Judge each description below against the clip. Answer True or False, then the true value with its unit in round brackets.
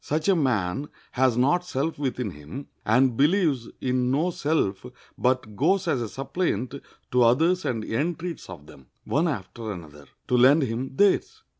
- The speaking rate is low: False (160 wpm)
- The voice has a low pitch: True (130 Hz)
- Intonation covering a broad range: True (5.7 semitones)